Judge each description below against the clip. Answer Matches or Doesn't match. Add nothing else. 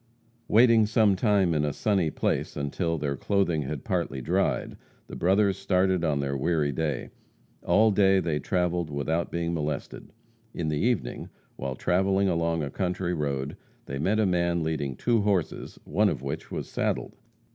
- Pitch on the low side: Matches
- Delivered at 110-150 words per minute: Doesn't match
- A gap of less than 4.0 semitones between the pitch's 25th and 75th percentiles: Doesn't match